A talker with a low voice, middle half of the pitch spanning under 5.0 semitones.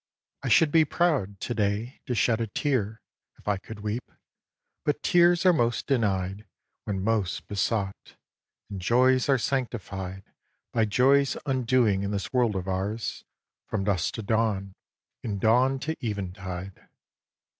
Yes: low, 110 Hz; average, 4.6 semitones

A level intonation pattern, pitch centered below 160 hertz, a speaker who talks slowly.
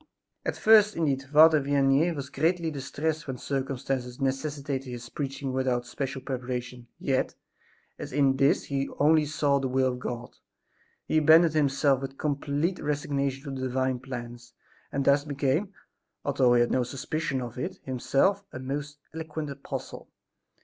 No: narrow, 2.2 semitones; medium, 140 Hz; average, 150 wpm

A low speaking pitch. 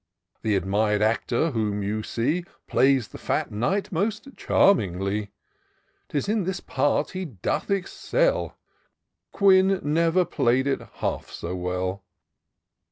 Yes: low, 130 Hz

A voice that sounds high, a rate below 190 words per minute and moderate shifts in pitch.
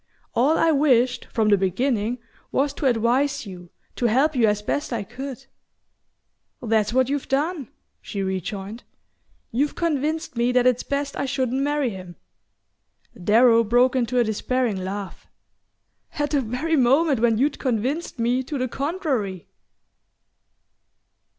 Yes: very high, 250 Hz; average, 145 wpm; average, 4.2 semitones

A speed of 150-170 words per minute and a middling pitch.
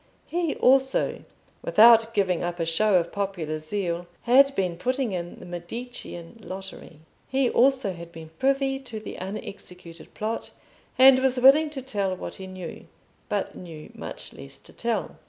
No: average, 155 wpm; high, 200 Hz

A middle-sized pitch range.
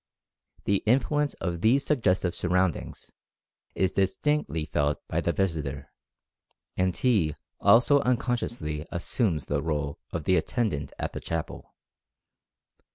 No: wide, 7.6 semitones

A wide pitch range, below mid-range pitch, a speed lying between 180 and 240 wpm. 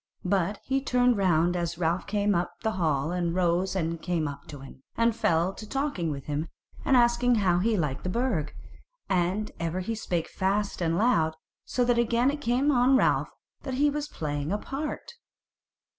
No: wide, 6.2 semitones; high, 190 Hz; average, 190 wpm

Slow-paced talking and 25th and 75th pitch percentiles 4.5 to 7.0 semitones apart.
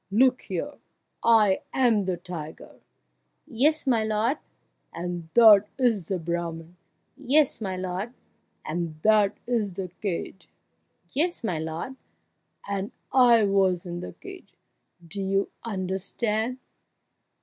Yes: slow, 125 wpm; average, 4.8 semitones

